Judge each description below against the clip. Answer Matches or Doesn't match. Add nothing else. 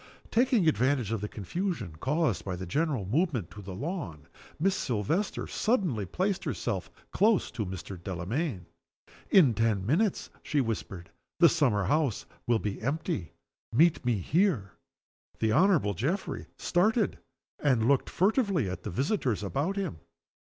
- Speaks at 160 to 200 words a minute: Doesn't match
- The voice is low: Matches